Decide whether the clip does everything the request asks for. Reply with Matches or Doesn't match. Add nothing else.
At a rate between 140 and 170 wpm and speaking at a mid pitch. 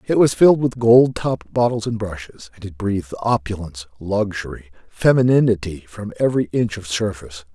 Doesn't match